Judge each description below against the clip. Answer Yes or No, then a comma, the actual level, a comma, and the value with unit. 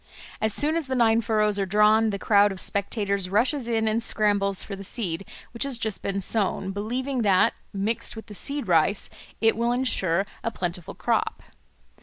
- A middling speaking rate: Yes, average, 185 wpm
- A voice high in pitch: Yes, high, 215 Hz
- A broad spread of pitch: No, average, 2.8 semitones